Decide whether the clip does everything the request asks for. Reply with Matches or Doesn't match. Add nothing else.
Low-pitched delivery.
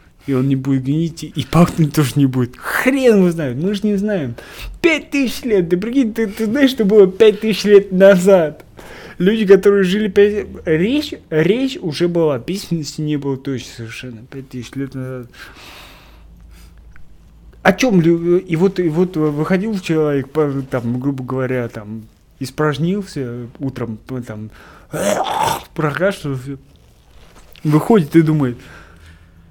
Doesn't match